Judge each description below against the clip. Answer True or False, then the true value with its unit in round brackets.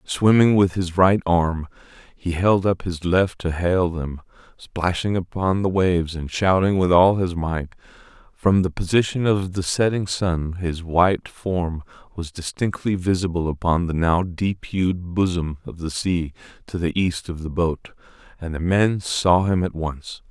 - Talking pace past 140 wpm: True (170 wpm)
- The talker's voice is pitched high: False (90 Hz)